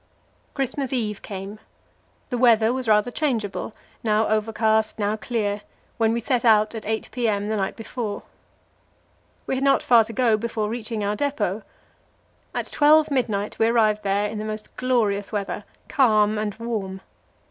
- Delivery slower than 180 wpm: Yes, average, 160 wpm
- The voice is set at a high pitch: Yes, high, 220 Hz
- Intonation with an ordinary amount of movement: No, narrow, 2.3 semitones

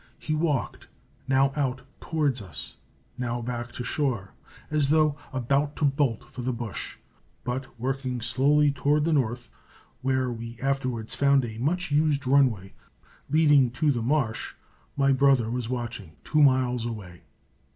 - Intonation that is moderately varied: Yes, average, 3.1 semitones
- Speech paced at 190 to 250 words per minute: No, average, 145 wpm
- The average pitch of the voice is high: No, low, 130 Hz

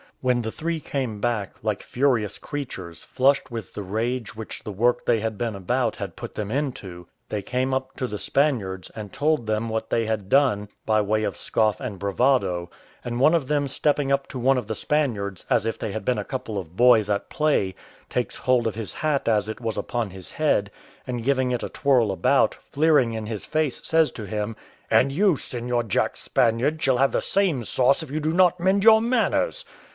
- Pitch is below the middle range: Yes, low, 120 Hz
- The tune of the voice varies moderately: Yes, average, 4.5 semitones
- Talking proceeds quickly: Yes, fast, 210 wpm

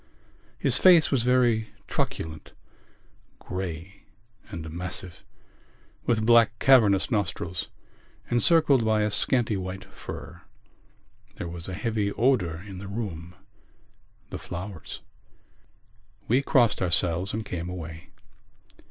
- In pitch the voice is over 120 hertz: No, low, 100 Hz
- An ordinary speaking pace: No, slow, 110 wpm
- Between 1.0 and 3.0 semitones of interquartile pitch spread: No, average, 4.8 semitones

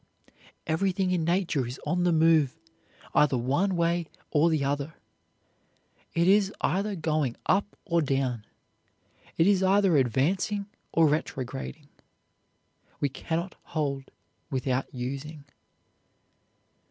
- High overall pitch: No, medium, 160 Hz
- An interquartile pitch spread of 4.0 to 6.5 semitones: Yes, average, 4.6 semitones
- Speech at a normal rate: No, slow, 110 wpm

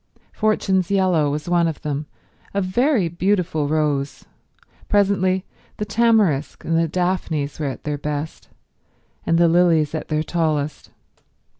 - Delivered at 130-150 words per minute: Yes, slow, 135 wpm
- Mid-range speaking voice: Yes, medium, 165 Hz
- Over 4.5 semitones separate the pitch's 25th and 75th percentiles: No, average, 3.8 semitones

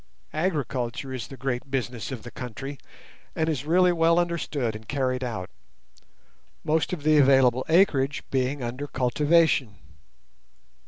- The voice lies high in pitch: No, low, 135 Hz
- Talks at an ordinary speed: No, slow, 130 wpm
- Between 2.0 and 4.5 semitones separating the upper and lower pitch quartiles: Yes, average, 3.8 semitones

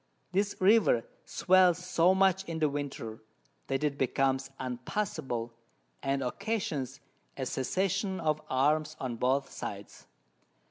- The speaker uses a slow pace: Yes, slow, 120 wpm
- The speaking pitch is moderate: Yes, medium, 150 Hz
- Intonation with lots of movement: Yes, wide, 5.9 semitones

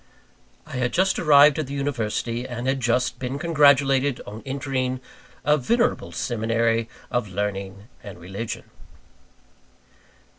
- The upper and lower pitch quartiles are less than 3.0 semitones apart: No, average, 3.7 semitones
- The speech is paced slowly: Yes, slow, 120 wpm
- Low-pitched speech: Yes, low, 125 Hz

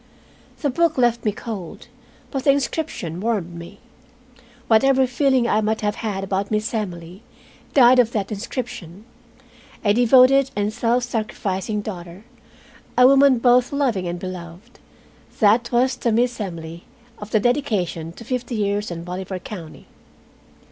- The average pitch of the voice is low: No, high, 215 Hz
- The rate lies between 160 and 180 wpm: No, average, 140 wpm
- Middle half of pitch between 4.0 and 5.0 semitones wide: Yes, average, 4.6 semitones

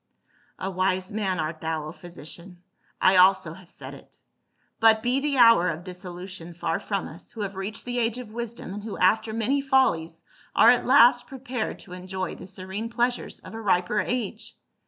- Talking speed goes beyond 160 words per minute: Yes, average, 185 wpm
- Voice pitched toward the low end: No, high, 195 Hz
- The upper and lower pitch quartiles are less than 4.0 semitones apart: No, average, 4.4 semitones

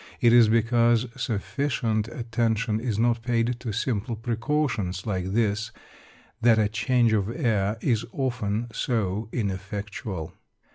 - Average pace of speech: No, slow, 125 wpm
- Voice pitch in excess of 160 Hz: No, low, 115 Hz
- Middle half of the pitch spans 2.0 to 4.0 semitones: Yes, narrow, 2.5 semitones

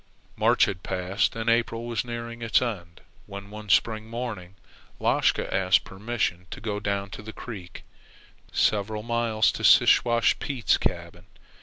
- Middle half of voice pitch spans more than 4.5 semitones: No, average, 3.2 semitones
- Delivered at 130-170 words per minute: Yes, average, 140 wpm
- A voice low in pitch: Yes, low, 110 Hz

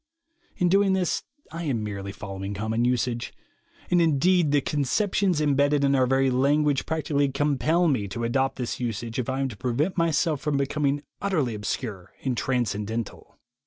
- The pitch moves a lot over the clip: No, average, 4.5 semitones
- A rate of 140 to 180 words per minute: Yes, average, 165 wpm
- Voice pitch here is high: No, low, 135 Hz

